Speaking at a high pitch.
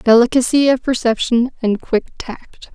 Yes: high, 240 Hz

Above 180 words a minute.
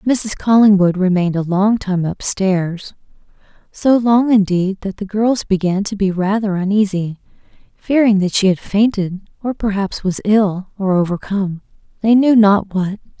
No: average, 145 wpm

